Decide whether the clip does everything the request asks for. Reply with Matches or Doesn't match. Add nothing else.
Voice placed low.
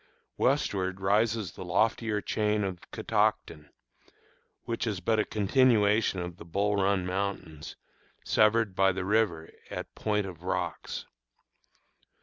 Matches